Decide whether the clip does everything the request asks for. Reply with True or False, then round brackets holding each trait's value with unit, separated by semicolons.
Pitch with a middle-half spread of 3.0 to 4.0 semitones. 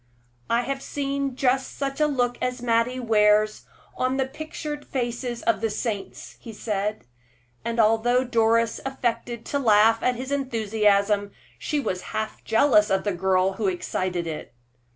True (3.5 semitones)